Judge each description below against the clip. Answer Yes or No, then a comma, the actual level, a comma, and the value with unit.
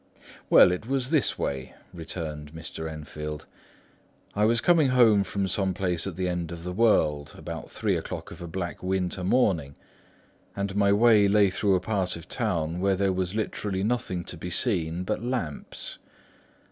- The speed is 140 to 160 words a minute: No, average, 170 wpm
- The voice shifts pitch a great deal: No, average, 3.7 semitones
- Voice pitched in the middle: No, very low, 95 Hz